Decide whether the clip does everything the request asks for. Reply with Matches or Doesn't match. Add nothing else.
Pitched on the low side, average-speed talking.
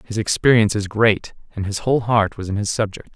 Doesn't match